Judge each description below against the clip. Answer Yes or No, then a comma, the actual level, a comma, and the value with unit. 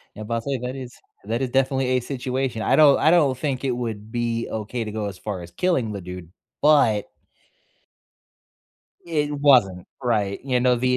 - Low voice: Yes, low, 125 Hz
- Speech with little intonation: No, average, 3.8 semitones